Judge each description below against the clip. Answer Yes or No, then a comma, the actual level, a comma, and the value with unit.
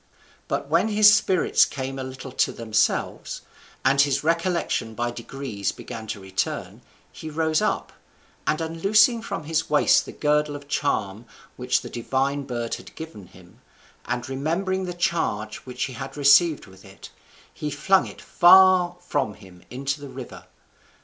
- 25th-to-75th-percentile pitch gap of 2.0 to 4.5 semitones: No, wide, 5.6 semitones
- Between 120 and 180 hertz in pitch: Yes, medium, 140 Hz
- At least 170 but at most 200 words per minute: No, average, 155 wpm